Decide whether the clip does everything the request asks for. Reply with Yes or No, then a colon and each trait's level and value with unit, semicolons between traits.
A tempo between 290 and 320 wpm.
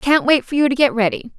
Yes: fast, 300 wpm